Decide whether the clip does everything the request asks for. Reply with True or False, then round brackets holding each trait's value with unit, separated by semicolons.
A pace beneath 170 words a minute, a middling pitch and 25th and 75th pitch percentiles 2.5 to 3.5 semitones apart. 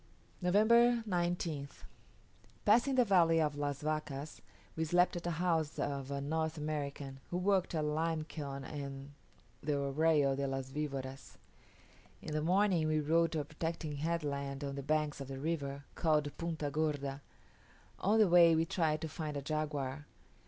True (160 wpm; 155 Hz; 2.9 semitones)